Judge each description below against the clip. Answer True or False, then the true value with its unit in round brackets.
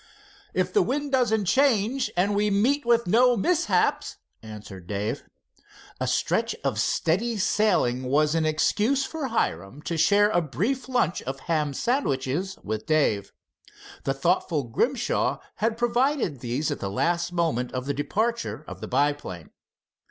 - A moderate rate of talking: True (145 wpm)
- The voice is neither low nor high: True (175 Hz)